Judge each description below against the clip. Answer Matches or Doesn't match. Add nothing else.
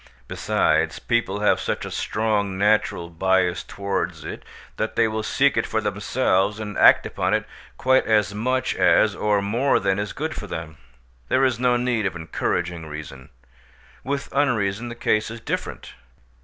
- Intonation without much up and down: Doesn't match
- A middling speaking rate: Matches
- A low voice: Matches